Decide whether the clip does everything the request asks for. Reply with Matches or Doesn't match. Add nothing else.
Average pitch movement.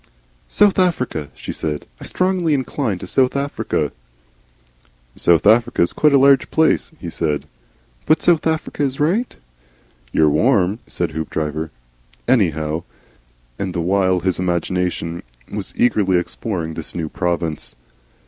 Doesn't match